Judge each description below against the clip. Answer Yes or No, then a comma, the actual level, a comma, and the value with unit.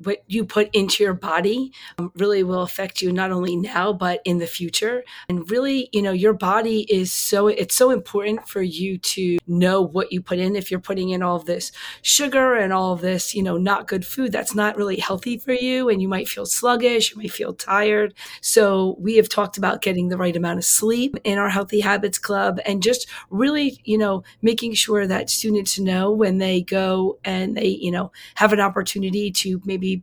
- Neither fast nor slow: No, fast, 215 wpm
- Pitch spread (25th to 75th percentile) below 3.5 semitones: Yes, narrow, 2.5 semitones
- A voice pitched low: No, high, 200 Hz